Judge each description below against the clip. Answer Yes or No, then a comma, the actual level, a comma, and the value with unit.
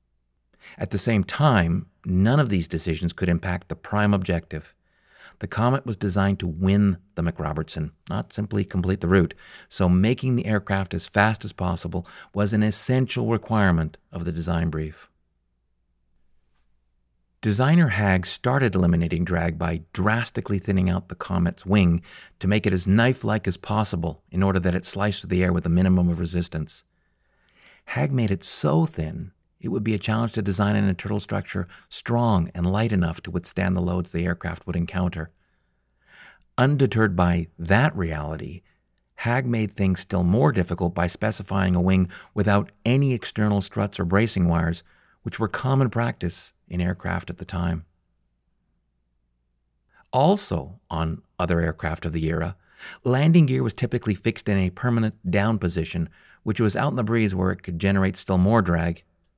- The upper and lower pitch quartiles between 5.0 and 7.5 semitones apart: No, average, 3.8 semitones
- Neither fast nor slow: Yes, average, 165 wpm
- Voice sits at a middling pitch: No, very low, 90 Hz